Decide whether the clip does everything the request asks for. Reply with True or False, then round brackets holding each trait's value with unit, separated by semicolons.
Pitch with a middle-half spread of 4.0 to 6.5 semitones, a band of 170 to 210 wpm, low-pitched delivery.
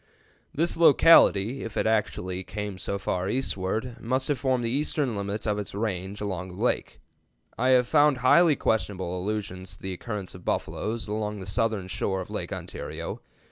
True (4.6 semitones; 180 wpm; 105 Hz)